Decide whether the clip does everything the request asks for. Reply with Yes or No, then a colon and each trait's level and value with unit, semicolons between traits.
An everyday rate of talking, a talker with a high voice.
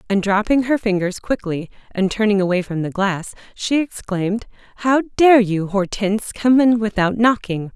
Yes: average, 160 wpm; high, 210 Hz